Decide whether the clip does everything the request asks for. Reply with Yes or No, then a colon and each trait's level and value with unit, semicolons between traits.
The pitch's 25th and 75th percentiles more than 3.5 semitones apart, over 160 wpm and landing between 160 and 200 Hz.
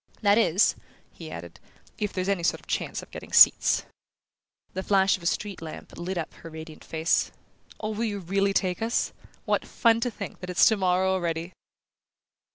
No: average, 2.9 semitones; average, 180 wpm; high, 190 Hz